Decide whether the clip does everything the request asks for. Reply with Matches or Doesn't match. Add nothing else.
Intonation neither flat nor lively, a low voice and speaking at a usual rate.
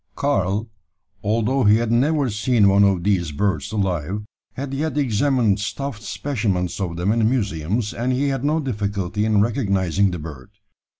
Matches